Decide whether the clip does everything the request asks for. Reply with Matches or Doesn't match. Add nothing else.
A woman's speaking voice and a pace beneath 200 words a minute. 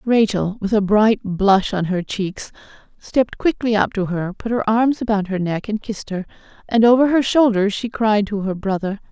Doesn't match